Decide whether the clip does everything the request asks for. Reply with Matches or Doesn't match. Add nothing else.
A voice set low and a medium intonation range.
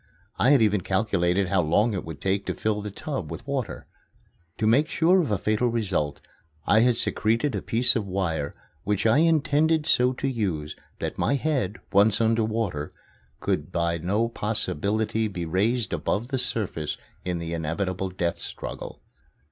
Matches